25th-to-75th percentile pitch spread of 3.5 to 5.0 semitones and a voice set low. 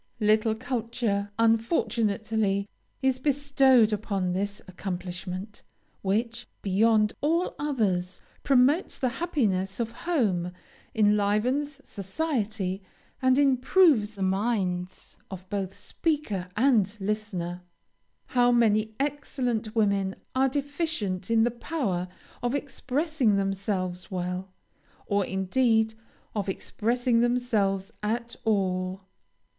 No: average, 4.5 semitones; high, 220 Hz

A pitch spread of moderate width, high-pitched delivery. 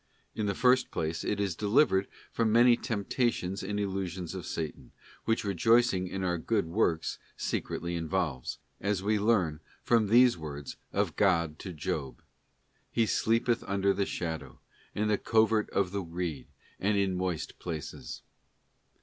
No: average, 4.0 semitones; very low, 95 Hz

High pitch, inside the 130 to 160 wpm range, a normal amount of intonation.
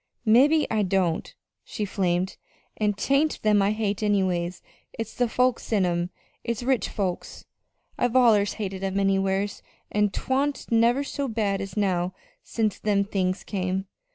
Yes: high, 205 Hz; average, 150 wpm; average, 3.1 semitones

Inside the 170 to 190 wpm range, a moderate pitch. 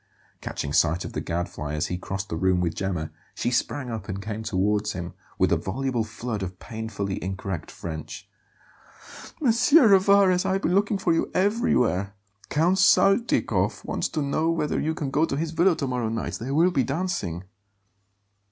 No: average, 180 wpm; low, 120 Hz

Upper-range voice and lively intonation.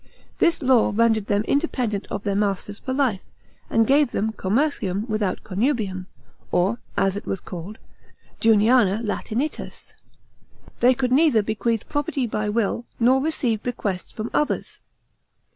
No: high, 225 Hz; average, 4.1 semitones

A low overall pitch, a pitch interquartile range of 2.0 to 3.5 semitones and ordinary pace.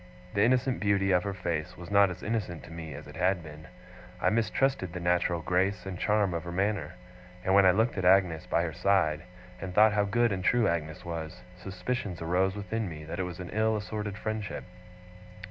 No: very low, 95 Hz; average, 3.1 semitones; fast, 210 wpm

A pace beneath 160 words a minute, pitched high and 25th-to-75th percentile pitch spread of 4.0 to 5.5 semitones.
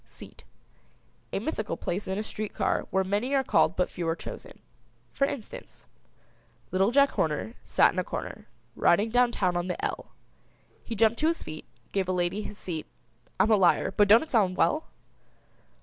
No: average, 185 wpm; high, 205 Hz; average, 4.6 semitones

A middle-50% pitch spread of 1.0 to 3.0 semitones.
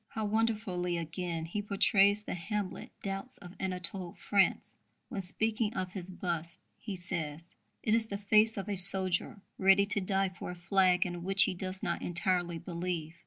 Yes: narrow, 2.5 semitones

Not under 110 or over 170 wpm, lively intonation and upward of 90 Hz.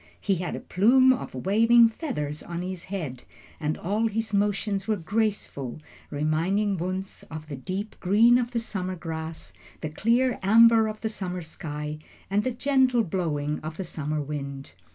Yes: average, 165 wpm; wide, 6.0 semitones; high, 190 Hz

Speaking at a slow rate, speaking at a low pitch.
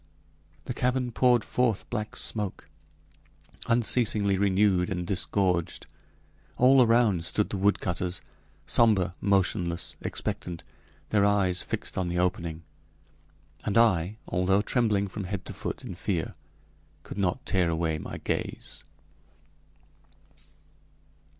Yes: slow, 110 wpm; low, 100 Hz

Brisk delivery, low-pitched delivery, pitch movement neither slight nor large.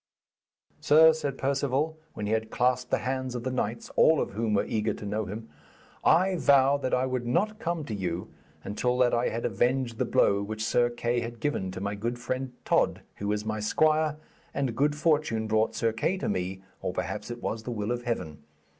Yes: fast, 210 wpm; low, 120 Hz; average, 4.0 semitones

